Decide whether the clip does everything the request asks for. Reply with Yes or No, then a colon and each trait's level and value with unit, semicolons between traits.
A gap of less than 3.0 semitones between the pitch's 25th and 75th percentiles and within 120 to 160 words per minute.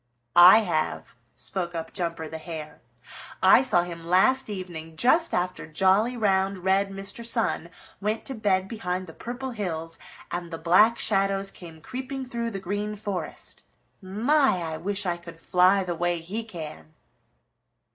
No: average, 3.9 semitones; average, 155 wpm